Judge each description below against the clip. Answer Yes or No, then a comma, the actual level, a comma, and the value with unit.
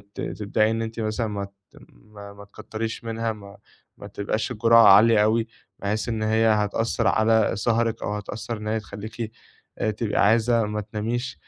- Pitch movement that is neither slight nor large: No, narrow, 1.4 semitones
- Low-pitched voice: Yes, low, 110 Hz